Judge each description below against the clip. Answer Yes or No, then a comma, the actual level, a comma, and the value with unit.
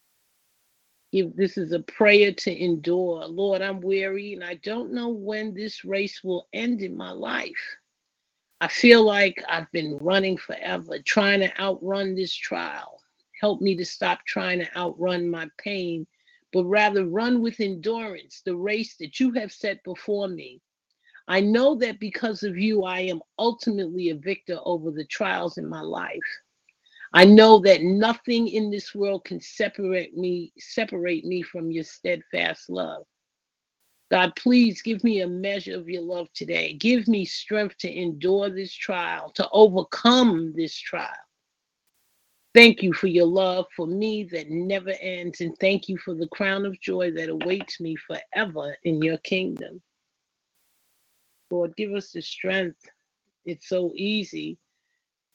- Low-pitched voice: No, high, 195 Hz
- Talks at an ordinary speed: Yes, average, 155 wpm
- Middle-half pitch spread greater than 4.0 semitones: No, average, 3.2 semitones